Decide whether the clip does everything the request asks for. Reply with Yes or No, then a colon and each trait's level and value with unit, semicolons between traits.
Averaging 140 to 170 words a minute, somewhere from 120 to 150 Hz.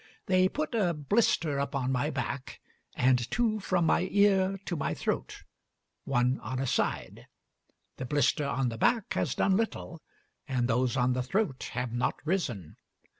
Yes: average, 160 wpm; medium, 140 Hz